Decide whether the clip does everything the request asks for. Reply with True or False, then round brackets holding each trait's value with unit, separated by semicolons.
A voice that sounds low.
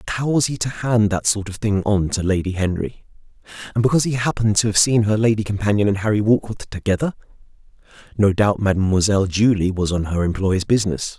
True (105 Hz)